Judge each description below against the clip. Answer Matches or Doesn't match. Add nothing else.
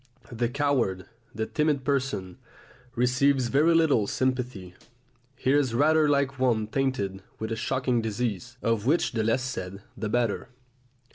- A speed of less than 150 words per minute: Matches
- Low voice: Matches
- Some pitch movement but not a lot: Matches